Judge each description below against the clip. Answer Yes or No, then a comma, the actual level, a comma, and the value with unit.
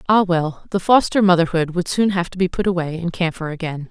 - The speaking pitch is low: No, medium, 175 Hz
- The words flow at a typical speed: No, fast, 230 wpm